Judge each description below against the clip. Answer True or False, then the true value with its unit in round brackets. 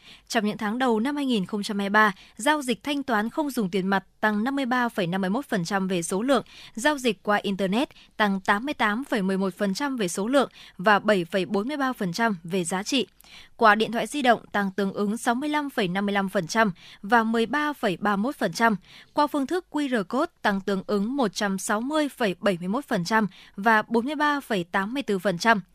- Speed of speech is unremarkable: False (130 wpm)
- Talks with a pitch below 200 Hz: False (215 Hz)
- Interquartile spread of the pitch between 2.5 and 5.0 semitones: True (4.2 semitones)